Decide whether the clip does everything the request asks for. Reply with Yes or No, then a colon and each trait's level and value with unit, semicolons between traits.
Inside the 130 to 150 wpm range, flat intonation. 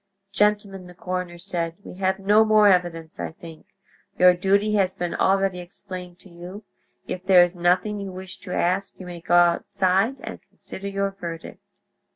No: average, 175 wpm; narrow, 2.0 semitones